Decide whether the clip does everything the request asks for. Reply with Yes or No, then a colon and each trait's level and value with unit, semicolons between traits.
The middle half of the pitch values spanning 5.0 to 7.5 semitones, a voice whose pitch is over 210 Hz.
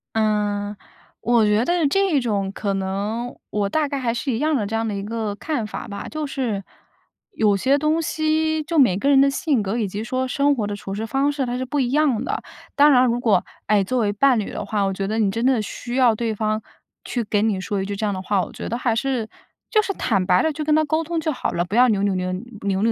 Yes: average, 5.3 semitones; high, 230 Hz